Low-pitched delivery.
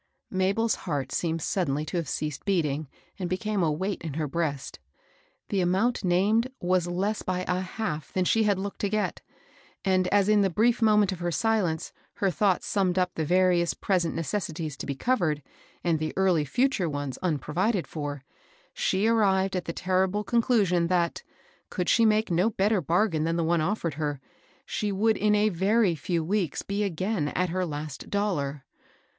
No: medium, 185 Hz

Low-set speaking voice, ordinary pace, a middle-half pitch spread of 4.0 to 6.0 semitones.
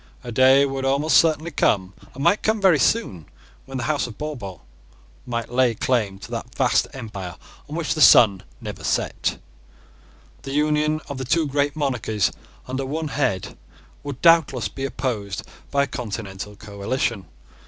Yes: low, 130 Hz; average, 155 wpm; average, 5.2 semitones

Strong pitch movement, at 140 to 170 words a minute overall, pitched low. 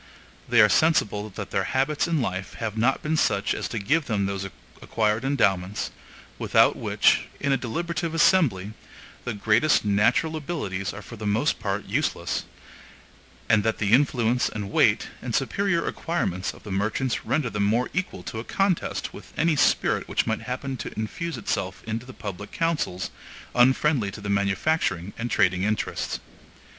Yes: wide, 6.4 semitones; average, 165 wpm; low, 115 Hz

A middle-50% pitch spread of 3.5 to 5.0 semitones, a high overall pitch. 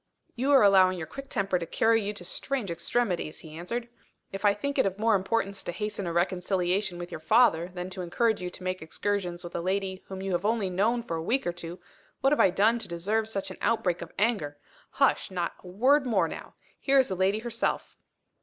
Yes: average, 4.2 semitones; high, 195 Hz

